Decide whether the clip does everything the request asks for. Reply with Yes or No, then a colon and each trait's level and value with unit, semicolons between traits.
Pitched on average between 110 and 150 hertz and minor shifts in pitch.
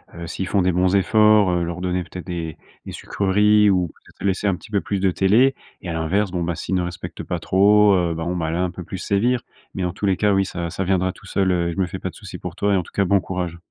No: very low, 95 Hz; narrow, 2.2 semitones